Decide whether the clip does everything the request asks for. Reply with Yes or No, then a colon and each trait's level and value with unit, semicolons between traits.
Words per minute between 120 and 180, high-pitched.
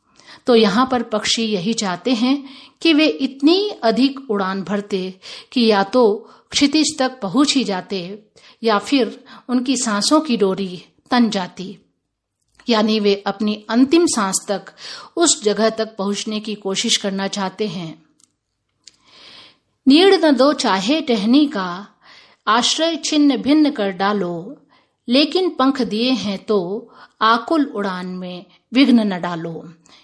Yes: average, 130 wpm; high, 225 Hz